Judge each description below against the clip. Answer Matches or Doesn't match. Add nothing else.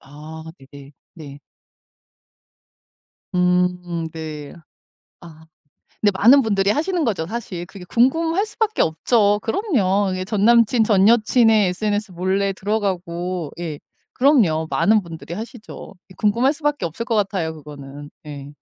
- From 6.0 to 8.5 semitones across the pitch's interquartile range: Doesn't match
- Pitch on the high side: Matches